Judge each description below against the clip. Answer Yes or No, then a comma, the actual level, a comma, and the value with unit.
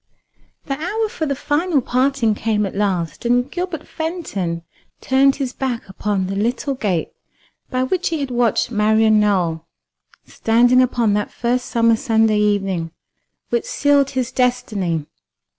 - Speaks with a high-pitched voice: Yes, high, 235 Hz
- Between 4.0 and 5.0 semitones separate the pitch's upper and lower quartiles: Yes, average, 4.7 semitones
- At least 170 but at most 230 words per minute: No, average, 140 wpm